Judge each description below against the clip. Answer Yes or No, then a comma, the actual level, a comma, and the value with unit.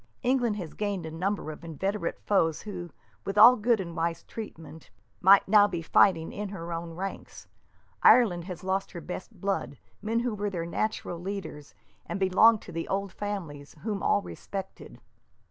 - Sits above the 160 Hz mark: Yes, high, 190 Hz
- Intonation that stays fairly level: No, average, 3.6 semitones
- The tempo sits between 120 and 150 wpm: No, average, 165 wpm